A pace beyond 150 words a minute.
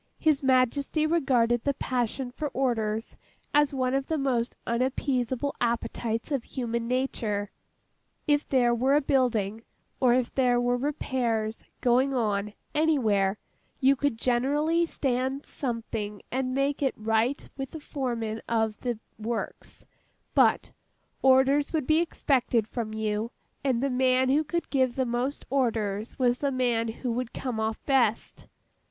No: average, 145 wpm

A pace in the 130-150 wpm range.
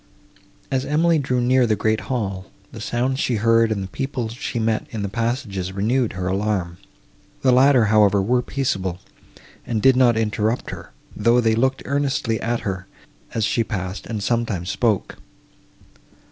No: average, 160 wpm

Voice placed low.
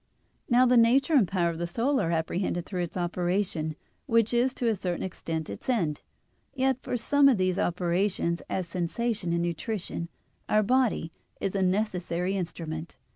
No: medium, 185 Hz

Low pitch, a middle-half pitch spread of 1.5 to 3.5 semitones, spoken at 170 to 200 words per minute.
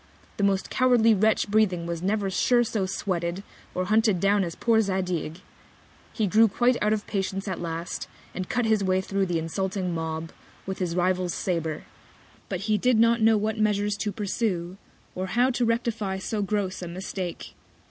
No: high, 195 Hz; average, 3.1 semitones; average, 180 wpm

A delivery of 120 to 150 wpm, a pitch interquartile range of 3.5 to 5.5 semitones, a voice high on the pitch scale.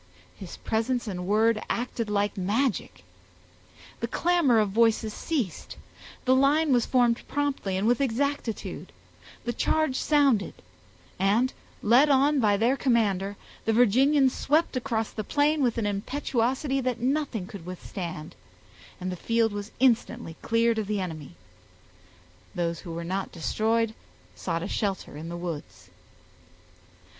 Yes: slow, 135 wpm; average, 5.0 semitones; high, 225 Hz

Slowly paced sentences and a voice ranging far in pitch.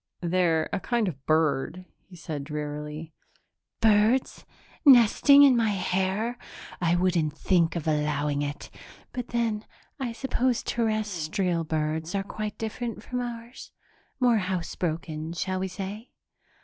Yes: slow, 125 wpm; wide, 6.2 semitones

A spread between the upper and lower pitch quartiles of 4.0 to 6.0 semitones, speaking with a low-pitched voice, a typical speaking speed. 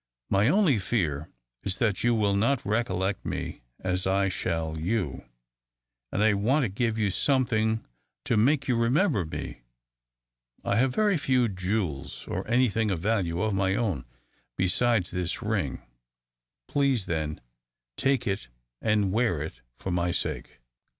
Yes: average, 4.6 semitones; low, 105 Hz; average, 150 wpm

